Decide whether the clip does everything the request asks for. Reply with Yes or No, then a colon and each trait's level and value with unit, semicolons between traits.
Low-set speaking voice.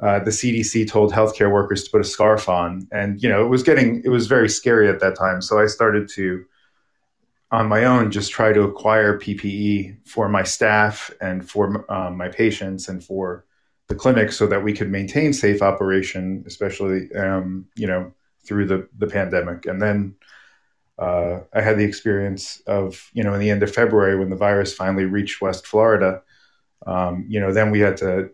Yes: low, 100 Hz